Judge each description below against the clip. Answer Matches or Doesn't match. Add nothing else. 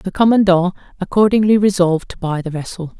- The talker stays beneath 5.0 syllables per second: Doesn't match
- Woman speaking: Matches